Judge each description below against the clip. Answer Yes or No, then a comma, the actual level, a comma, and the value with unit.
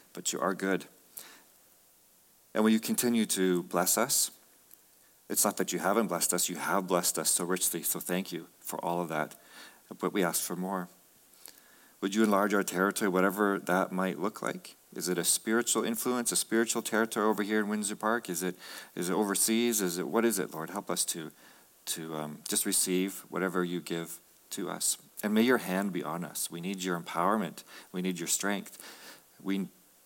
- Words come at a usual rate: Yes, average, 195 wpm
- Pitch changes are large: No, average, 3.1 semitones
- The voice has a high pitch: No, very low, 95 Hz